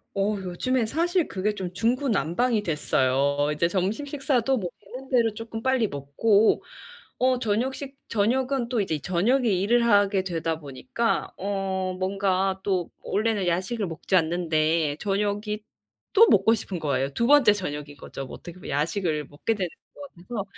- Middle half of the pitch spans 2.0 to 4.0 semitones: No, average, 5.3 semitones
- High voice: Yes, high, 200 Hz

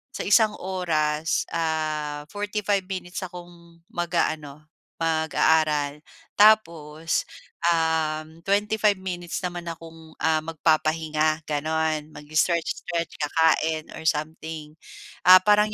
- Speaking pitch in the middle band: Yes, medium, 160 Hz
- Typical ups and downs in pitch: No, narrow, 2.2 semitones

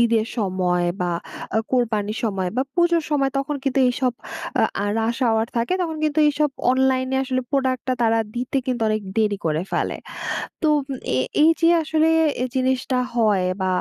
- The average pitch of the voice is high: Yes, very high, 250 Hz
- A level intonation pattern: No, average, 4.0 semitones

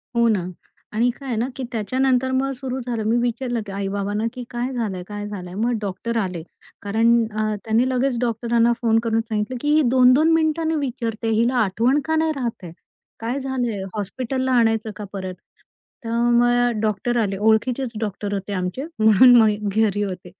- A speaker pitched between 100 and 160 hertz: No, high, 230 Hz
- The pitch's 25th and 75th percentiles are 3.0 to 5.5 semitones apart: Yes, average, 3.3 semitones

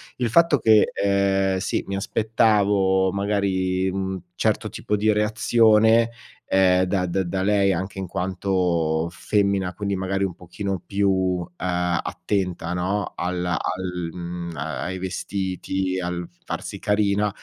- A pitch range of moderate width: No, narrow, 1.9 semitones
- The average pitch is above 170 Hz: No, very low, 95 Hz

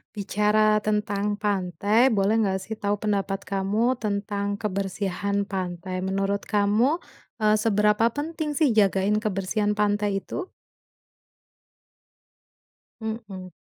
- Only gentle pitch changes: Yes, narrow, 1.6 semitones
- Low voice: No, high, 205 Hz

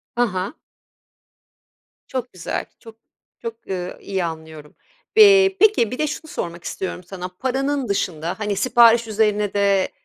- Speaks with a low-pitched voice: No, high, 210 Hz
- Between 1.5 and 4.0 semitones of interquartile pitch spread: No, wide, 5.6 semitones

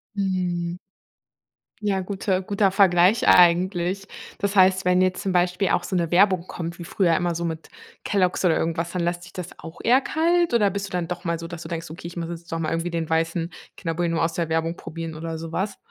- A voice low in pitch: No, medium, 175 Hz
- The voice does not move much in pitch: Yes, narrow, 2.2 semitones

